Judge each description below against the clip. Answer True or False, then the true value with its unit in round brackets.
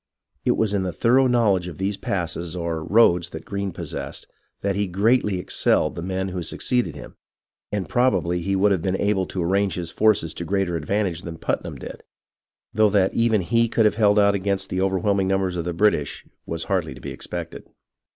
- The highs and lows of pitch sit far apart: False (2.9 semitones)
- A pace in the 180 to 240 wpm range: True (200 wpm)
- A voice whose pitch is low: True (95 Hz)